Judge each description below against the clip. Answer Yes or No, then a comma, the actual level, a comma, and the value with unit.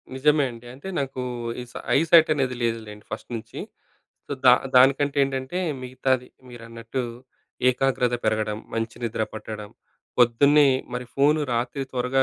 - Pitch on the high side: No, low, 125 Hz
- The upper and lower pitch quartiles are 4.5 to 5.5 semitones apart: No, average, 2.9 semitones